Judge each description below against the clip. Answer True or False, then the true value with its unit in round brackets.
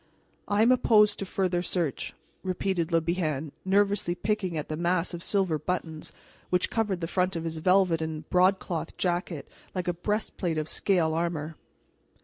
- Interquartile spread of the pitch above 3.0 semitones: False (2.7 semitones)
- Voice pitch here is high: False (175 Hz)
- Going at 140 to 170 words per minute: True (160 wpm)